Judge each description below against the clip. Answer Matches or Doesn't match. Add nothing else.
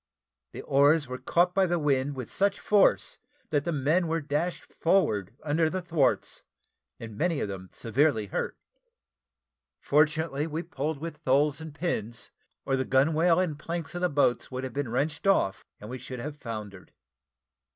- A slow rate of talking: Doesn't match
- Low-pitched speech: Doesn't match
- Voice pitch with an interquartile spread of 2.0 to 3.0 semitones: Doesn't match